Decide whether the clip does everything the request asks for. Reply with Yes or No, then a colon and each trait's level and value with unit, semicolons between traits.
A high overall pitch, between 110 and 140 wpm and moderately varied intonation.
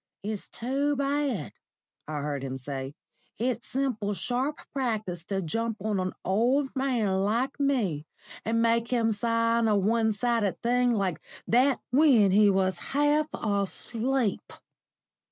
Yes: high, 230 Hz; slow, 135 wpm; average, 4.5 semitones